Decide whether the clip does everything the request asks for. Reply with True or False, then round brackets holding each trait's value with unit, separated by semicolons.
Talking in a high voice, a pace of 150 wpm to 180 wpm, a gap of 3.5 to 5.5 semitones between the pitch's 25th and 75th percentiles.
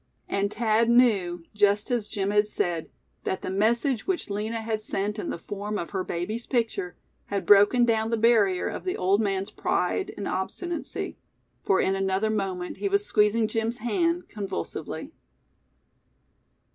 False (210 Hz; 160 wpm; 2.9 semitones)